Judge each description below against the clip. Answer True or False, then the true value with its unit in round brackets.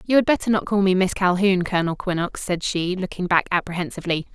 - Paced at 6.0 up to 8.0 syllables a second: True (6.4 syllables/s)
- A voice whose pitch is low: False (185 Hz)